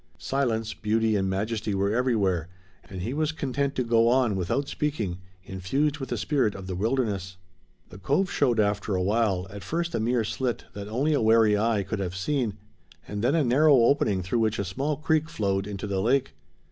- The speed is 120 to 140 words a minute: No, average, 195 wpm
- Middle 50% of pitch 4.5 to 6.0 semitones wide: Yes, average, 5.2 semitones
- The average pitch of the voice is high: No, low, 110 Hz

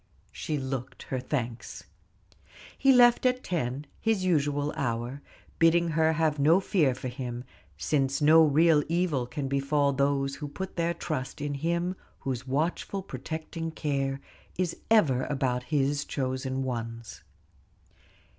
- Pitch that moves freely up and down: No, average, 3.8 semitones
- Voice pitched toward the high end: No, medium, 145 Hz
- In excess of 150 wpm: No, slow, 135 wpm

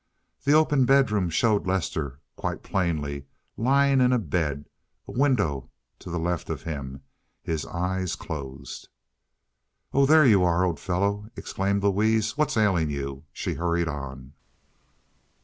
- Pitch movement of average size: No, wide, 6.6 semitones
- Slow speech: Yes, slow, 130 wpm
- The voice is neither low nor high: No, very low, 90 Hz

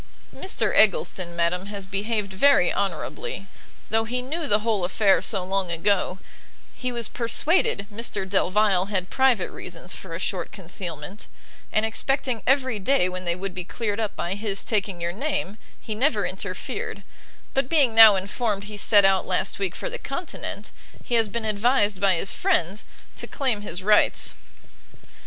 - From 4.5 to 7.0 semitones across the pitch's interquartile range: No, average, 3.7 semitones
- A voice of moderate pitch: No, high, 205 Hz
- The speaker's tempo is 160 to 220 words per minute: Yes, average, 165 wpm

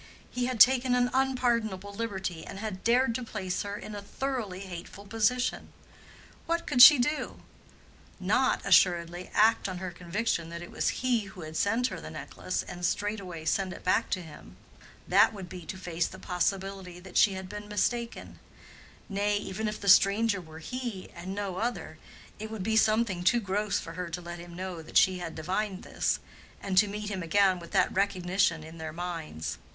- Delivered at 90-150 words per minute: No, average, 190 wpm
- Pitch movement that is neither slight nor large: Yes, average, 3.6 semitones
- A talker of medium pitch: No, high, 195 Hz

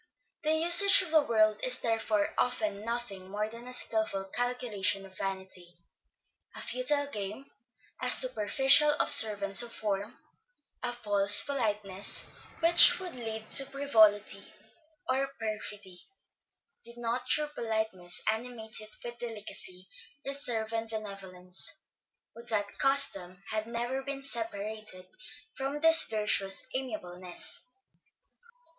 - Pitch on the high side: Yes, high, 220 Hz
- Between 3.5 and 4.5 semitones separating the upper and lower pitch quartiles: Yes, average, 4.0 semitones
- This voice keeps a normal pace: No, slow, 115 wpm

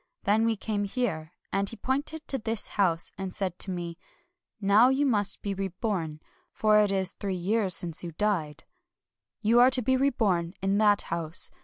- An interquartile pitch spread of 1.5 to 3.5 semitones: No, average, 4.0 semitones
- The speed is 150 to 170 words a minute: No, average, 195 wpm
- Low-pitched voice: No, high, 205 Hz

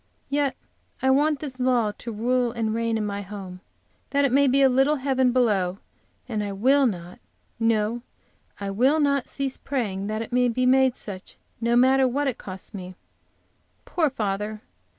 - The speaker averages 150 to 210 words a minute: Yes, average, 170 wpm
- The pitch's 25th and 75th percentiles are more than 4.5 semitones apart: No, average, 4.2 semitones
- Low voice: No, high, 240 Hz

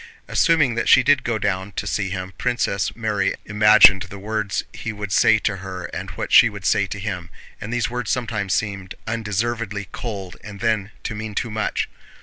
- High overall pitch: No, low, 105 Hz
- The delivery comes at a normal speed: Yes, average, 190 wpm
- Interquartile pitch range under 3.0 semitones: Yes, narrow, 2.4 semitones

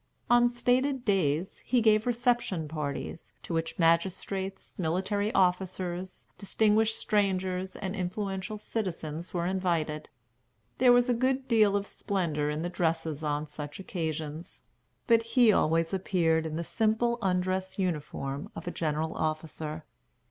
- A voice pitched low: No, medium, 185 Hz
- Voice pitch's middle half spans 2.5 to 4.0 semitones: No, average, 4.8 semitones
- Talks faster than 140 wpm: No, slow, 135 wpm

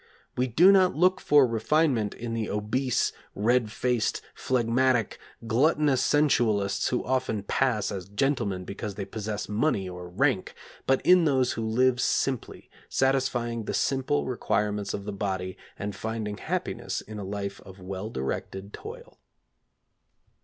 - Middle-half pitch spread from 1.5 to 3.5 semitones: No, average, 4.5 semitones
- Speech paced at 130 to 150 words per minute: Yes, average, 140 wpm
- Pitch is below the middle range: Yes, low, 115 Hz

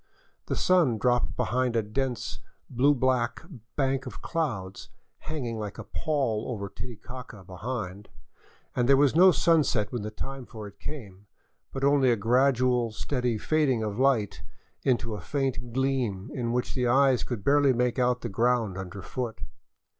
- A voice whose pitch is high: No, low, 125 Hz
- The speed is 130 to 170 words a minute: Yes, average, 155 wpm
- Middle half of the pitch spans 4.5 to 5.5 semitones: No, average, 3.6 semitones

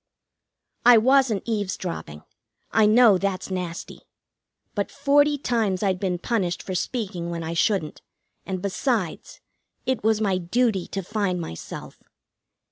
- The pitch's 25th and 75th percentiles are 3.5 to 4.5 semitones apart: Yes, average, 4.2 semitones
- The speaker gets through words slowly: Yes, slow, 125 wpm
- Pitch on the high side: Yes, high, 200 Hz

